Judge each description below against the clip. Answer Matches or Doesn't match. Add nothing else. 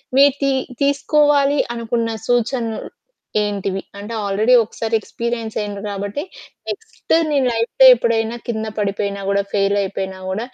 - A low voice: Doesn't match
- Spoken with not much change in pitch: Doesn't match